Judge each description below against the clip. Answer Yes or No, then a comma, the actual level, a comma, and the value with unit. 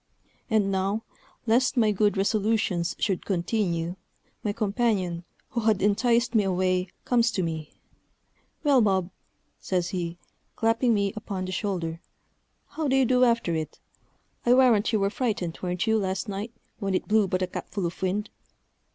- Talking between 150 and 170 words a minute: Yes, average, 160 wpm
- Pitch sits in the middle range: No, high, 200 Hz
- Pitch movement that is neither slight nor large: Yes, average, 3.6 semitones